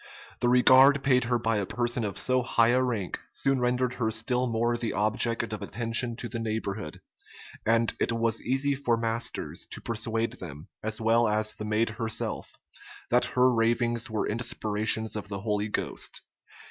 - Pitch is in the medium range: No, low, 115 Hz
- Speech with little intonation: Yes, narrow, 2.1 semitones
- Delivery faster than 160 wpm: Yes, average, 170 wpm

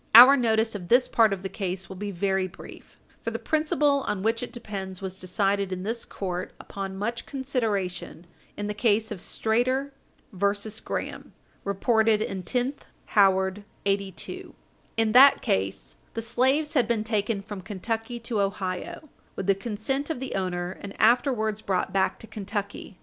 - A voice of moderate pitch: No, high, 210 Hz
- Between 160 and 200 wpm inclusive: Yes, average, 170 wpm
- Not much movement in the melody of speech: No, average, 3.6 semitones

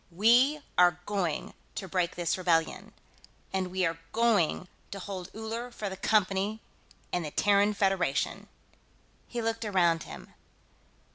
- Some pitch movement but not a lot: Yes, average, 3.5 semitones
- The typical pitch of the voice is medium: No, high, 195 Hz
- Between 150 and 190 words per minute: No, slow, 135 wpm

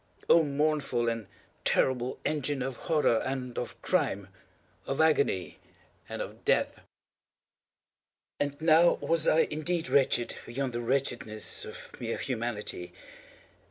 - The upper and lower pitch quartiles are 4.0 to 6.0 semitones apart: Yes, average, 4.4 semitones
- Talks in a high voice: No, low, 135 Hz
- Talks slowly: Yes, slow, 115 wpm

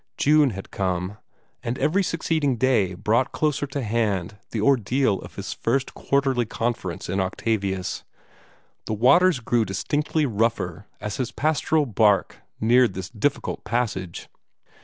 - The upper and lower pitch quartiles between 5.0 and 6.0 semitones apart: Yes, wide, 5.5 semitones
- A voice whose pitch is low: Yes, low, 115 Hz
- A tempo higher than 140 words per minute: No, slow, 135 wpm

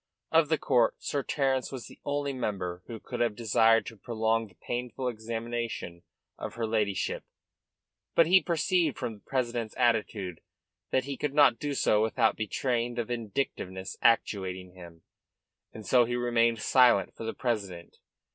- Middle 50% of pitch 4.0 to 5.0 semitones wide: No, average, 3.3 semitones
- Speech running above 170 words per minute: No, average, 155 wpm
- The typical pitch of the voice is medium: No, low, 115 Hz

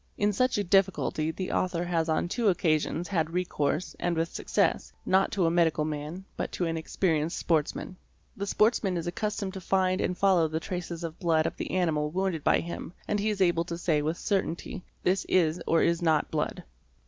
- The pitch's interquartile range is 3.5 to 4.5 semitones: No, average, 2.7 semitones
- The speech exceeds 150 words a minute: Yes, fast, 205 wpm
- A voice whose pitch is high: No, medium, 175 Hz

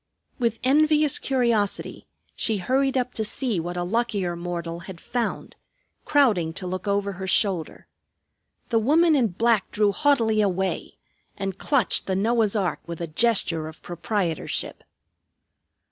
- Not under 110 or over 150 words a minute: Yes, average, 140 wpm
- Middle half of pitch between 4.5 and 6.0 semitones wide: Yes, average, 5.2 semitones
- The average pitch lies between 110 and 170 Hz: No, high, 205 Hz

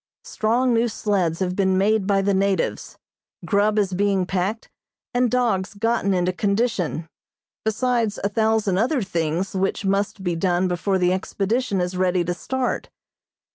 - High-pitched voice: Yes, high, 195 Hz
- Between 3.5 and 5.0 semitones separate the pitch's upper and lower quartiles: No, average, 3.0 semitones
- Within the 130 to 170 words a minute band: Yes, average, 150 wpm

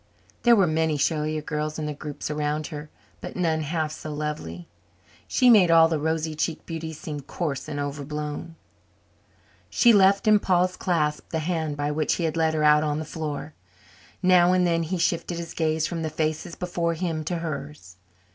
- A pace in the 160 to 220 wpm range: Yes, average, 190 wpm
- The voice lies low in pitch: No, medium, 160 Hz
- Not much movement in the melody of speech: Yes, narrow, 2.1 semitones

